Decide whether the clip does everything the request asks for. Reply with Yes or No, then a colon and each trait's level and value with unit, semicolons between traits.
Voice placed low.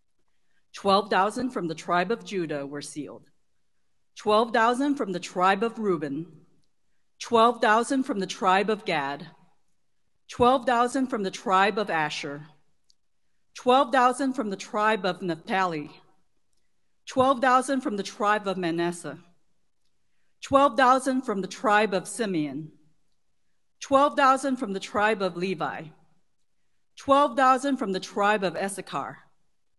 No: high, 195 Hz